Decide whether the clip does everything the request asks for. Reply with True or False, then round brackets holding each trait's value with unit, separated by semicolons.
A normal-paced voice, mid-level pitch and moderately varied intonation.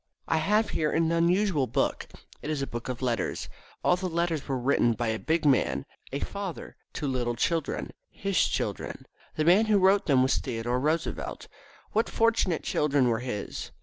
False (180 wpm; 155 Hz; 5.8 semitones)